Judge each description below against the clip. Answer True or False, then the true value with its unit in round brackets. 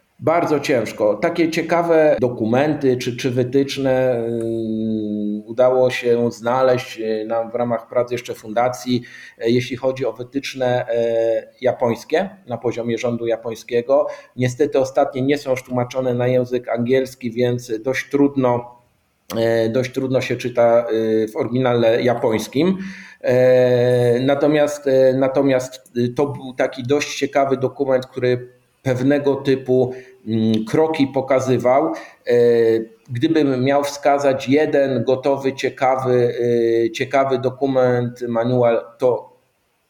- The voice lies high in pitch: False (125 Hz)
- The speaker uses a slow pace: True (100 wpm)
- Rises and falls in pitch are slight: True (2.3 semitones)